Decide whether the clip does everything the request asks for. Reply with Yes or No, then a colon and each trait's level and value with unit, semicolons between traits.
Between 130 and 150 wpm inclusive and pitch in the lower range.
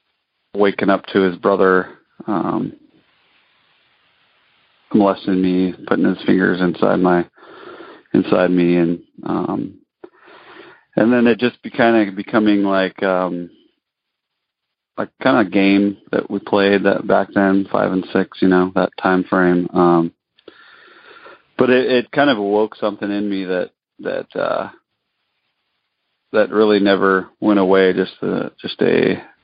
Yes: slow, 135 wpm; very low, 95 Hz